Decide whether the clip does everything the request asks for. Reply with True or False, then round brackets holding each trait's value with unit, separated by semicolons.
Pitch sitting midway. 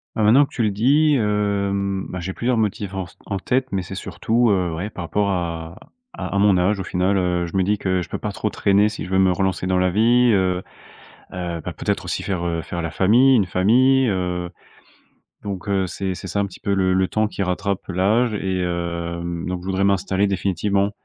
False (95 Hz)